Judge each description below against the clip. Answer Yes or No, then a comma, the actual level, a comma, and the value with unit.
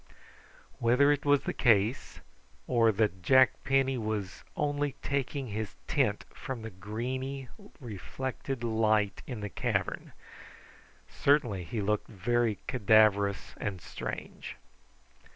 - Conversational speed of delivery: No, slow, 115 wpm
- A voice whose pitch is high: No, low, 115 Hz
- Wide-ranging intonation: No, average, 4.2 semitones